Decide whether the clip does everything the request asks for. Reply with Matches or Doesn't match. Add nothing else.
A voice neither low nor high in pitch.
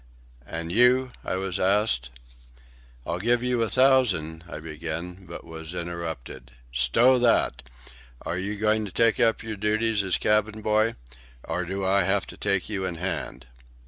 Doesn't match